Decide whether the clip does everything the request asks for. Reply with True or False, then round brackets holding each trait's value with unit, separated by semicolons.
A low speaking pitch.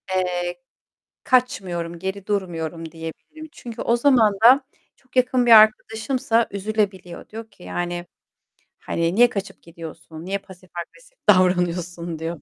False (190 Hz)